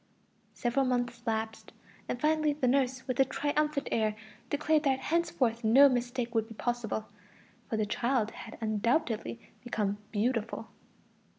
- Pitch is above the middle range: Yes, high, 245 Hz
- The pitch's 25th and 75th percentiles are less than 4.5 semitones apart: Yes, average, 3.5 semitones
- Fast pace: No, slow, 135 wpm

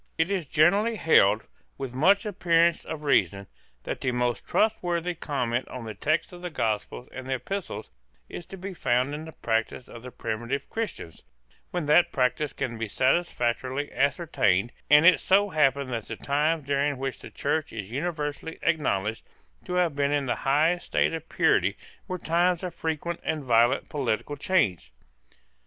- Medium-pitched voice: Yes, medium, 145 Hz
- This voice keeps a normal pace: Yes, average, 165 wpm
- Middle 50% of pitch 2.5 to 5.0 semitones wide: No, wide, 5.6 semitones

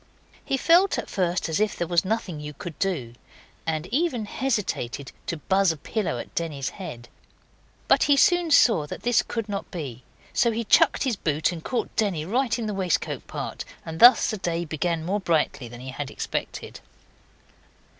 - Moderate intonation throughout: No, wide, 6.4 semitones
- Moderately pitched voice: Yes, medium, 180 Hz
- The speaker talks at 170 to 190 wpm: Yes, average, 185 wpm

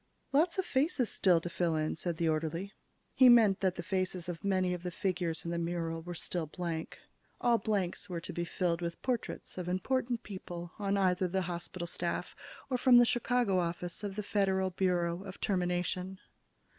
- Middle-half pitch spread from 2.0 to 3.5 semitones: Yes, average, 2.8 semitones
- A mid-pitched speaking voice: Yes, medium, 180 Hz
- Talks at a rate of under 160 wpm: No, average, 190 wpm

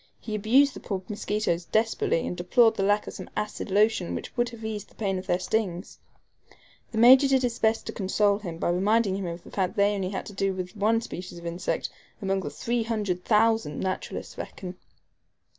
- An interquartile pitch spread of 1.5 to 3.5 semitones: Yes, average, 3.1 semitones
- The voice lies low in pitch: No, high, 205 Hz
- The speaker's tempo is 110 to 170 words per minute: No, fast, 205 wpm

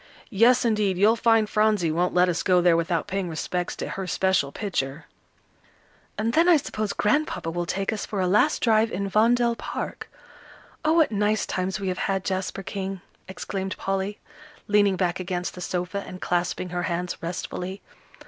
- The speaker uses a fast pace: No, average, 175 wpm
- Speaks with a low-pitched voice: No, high, 195 Hz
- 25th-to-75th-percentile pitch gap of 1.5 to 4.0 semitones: Yes, average, 3.0 semitones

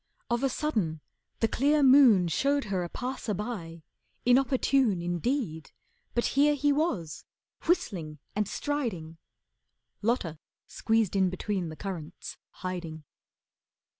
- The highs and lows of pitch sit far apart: Yes, wide, 7.7 semitones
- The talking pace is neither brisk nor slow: No, slow, 115 wpm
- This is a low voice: No, high, 210 Hz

